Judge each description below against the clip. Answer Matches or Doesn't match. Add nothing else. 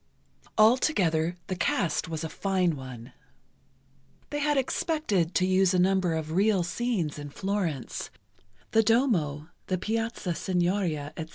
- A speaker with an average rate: Doesn't match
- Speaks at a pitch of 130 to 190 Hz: Matches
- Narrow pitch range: Doesn't match